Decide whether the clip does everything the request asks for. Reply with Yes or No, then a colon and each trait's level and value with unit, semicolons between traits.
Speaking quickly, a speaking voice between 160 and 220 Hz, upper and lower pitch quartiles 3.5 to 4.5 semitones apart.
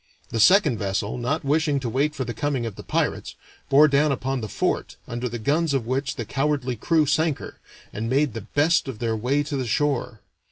No: fast, 215 wpm; low, 135 Hz; average, 3.9 semitones